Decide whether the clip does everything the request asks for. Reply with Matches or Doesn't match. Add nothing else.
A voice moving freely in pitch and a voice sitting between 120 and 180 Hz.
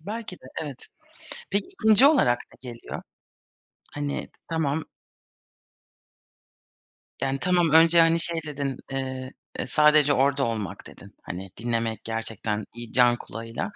Matches